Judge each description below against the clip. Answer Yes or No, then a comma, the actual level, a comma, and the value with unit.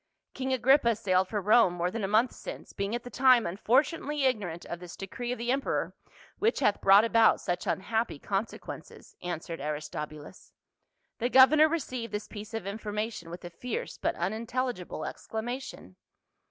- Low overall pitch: No, high, 220 Hz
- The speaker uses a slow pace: No, average, 165 wpm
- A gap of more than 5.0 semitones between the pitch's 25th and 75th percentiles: Yes, wide, 5.4 semitones